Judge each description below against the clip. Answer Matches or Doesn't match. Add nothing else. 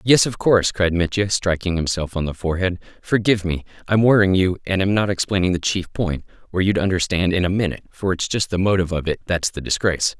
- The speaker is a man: Matches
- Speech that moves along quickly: Matches